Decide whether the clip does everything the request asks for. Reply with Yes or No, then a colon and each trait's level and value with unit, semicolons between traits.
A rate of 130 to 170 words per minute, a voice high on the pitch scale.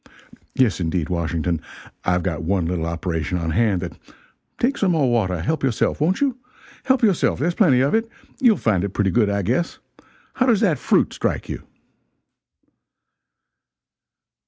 No: average, 160 wpm; low, 105 Hz